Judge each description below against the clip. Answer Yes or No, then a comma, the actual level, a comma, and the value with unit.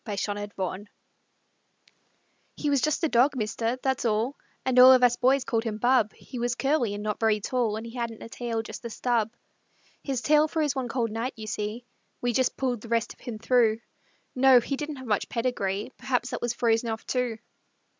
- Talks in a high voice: Yes, high, 240 Hz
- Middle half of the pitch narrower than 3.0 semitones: Yes, narrow, 2.6 semitones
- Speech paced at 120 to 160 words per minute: No, fast, 205 wpm